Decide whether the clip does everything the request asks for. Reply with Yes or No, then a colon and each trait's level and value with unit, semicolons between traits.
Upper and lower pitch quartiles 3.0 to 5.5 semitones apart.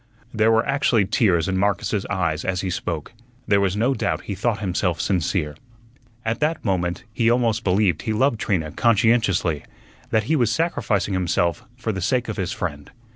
Yes: average, 4.2 semitones